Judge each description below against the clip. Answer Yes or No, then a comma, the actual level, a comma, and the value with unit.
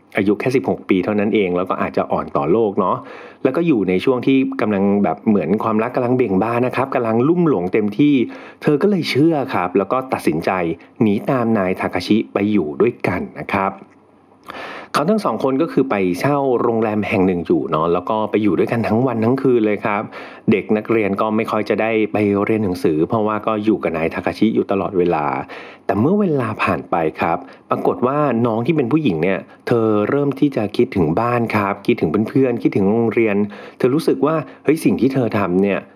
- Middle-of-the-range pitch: No, low, 110 Hz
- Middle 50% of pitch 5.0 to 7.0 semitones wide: No, average, 3.7 semitones